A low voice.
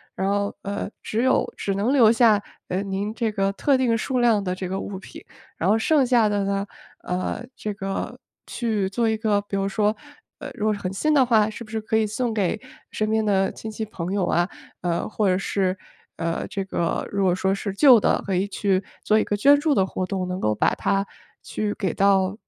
No: high, 205 Hz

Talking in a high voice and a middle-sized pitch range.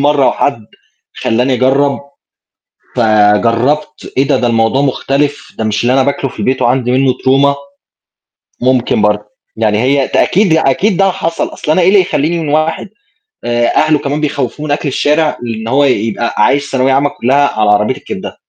No: low, 135 Hz; average, 3.6 semitones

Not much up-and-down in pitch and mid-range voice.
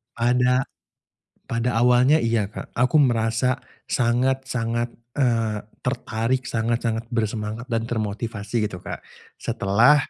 No: narrow, 2.0 semitones; low, 115 Hz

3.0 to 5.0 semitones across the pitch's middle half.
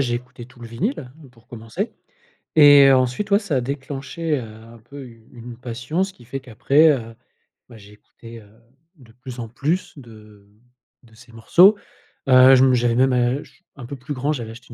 Yes: average, 3.4 semitones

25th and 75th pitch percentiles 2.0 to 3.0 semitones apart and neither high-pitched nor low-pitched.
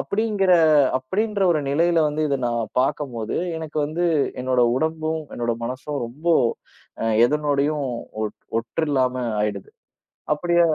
No: average, 4.3 semitones; medium, 150 Hz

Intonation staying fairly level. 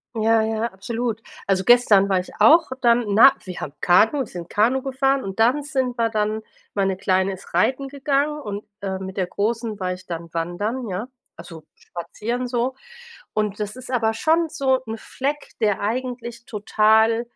No: average, 4.5 semitones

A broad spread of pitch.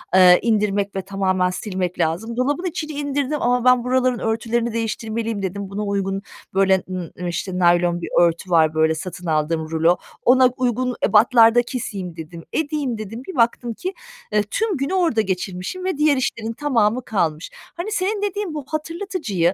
Yes: wide, 6.0 semitones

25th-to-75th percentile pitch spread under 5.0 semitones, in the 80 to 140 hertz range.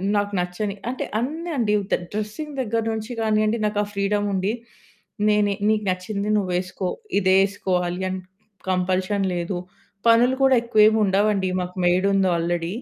No: narrow, 2.6 semitones; high, 205 Hz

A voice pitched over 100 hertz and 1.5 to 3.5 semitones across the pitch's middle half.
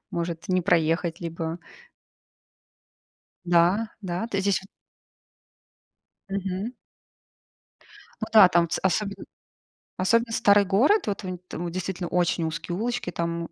Yes: medium, 185 Hz; average, 3.0 semitones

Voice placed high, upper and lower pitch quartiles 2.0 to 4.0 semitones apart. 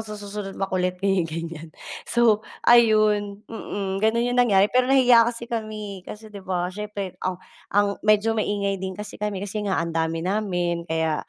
Yes: high, 205 Hz; average, 2.7 semitones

